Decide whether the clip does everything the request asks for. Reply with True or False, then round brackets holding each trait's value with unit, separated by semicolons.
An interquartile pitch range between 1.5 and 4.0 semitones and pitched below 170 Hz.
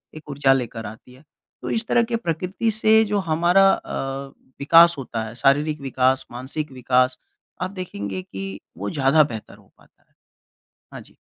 False (5.1 semitones; 135 Hz)